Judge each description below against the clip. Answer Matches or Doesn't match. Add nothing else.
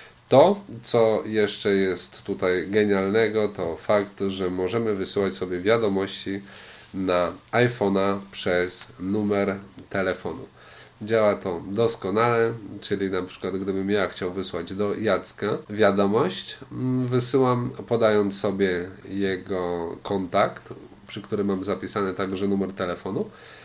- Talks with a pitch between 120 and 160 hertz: Doesn't match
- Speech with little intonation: Matches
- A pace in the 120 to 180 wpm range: Doesn't match